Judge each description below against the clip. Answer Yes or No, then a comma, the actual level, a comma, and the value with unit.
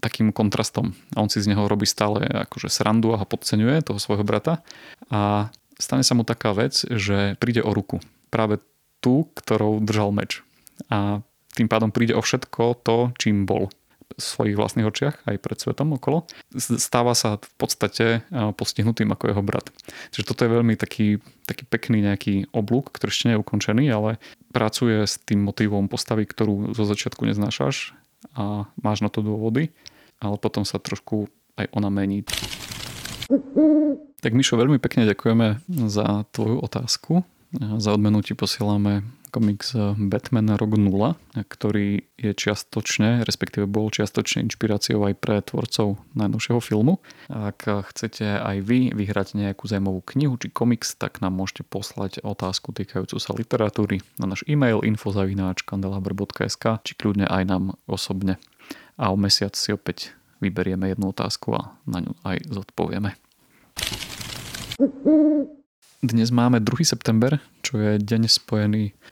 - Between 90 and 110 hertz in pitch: Yes, low, 105 Hz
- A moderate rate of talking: Yes, average, 145 wpm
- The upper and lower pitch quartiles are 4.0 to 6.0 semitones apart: No, average, 2.7 semitones